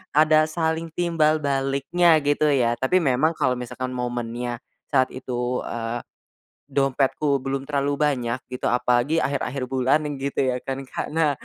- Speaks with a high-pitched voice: No, low, 135 Hz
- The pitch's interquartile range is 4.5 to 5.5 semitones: No, average, 3.3 semitones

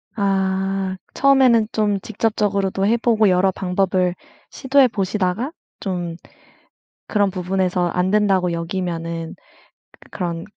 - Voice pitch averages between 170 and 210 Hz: Yes, high, 190 Hz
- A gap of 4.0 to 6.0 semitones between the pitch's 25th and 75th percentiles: No, average, 2.7 semitones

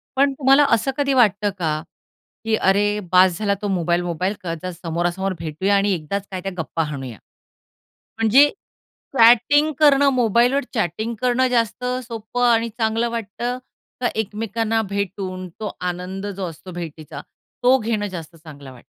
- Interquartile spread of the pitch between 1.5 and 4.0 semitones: No, average, 4.7 semitones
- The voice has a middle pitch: No, high, 205 Hz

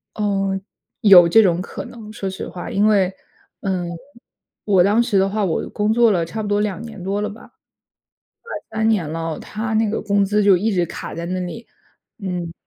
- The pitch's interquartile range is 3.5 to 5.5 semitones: No, average, 2.9 semitones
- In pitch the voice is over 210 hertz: No, high, 200 Hz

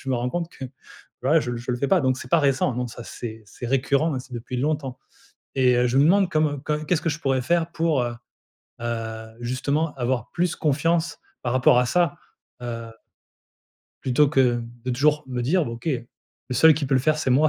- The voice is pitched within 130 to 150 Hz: Yes, low, 135 Hz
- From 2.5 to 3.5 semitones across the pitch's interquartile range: No, average, 4.0 semitones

